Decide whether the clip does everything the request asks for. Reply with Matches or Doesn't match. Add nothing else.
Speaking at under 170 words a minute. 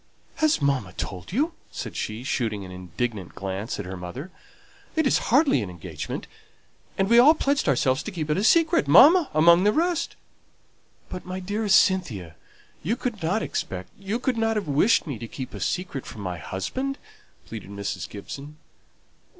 Doesn't match